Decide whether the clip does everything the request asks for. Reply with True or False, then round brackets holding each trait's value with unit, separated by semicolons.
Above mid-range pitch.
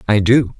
False (110 Hz)